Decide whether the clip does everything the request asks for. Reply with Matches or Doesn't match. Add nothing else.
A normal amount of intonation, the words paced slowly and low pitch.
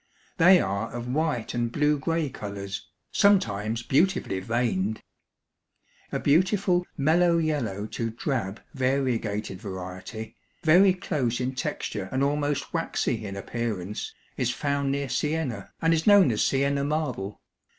Doesn't match